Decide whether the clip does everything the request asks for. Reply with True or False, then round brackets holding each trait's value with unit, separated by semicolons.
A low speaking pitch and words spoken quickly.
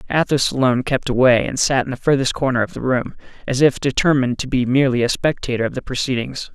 True (130 Hz; 220 wpm)